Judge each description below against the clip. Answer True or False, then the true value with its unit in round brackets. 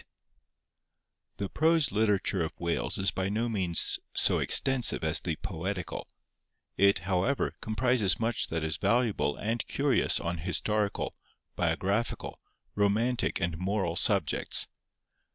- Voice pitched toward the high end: False (100 Hz)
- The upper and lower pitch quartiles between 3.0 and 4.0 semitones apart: False (4.4 semitones)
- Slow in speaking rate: True (115 wpm)